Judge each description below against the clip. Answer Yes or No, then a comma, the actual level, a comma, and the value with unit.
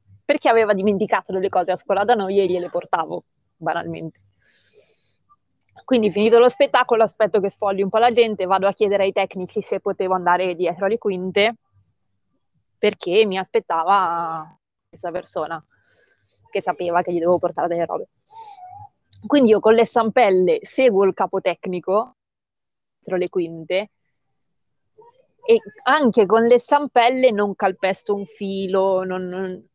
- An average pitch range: Yes, average, 3.9 semitones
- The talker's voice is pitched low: No, high, 195 Hz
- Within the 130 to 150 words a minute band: Yes, average, 145 wpm